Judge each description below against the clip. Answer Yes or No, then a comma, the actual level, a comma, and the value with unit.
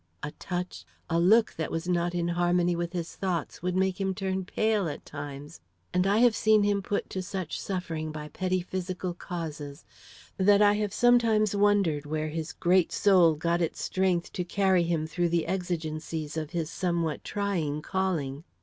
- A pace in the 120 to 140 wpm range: No, average, 175 wpm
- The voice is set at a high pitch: No, medium, 175 Hz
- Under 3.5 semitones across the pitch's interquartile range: Yes, average, 2.9 semitones